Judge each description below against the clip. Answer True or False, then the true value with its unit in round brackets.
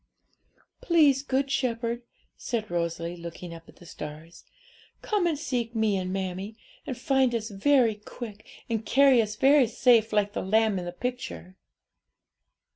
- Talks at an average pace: True (150 wpm)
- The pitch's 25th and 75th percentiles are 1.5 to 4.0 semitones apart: False (5.4 semitones)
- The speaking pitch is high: True (220 Hz)